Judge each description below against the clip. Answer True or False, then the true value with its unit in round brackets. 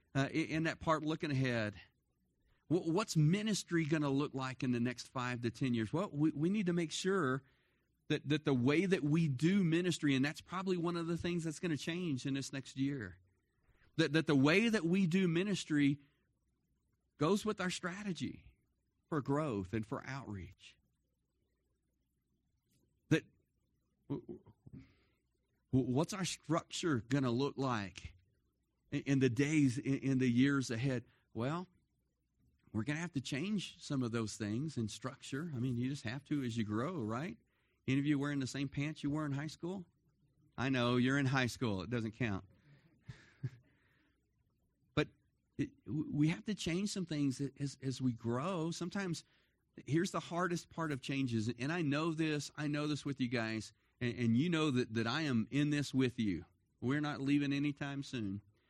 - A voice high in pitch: False (140 Hz)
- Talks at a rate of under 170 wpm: False (175 wpm)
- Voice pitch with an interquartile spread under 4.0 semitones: False (4.5 semitones)